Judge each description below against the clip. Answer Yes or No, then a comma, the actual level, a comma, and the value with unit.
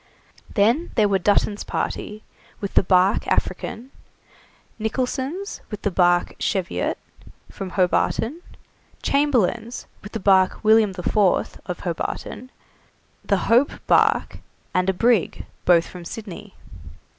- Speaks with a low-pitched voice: No, high, 205 Hz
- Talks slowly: Yes, slow, 120 wpm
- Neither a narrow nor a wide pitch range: Yes, average, 4.1 semitones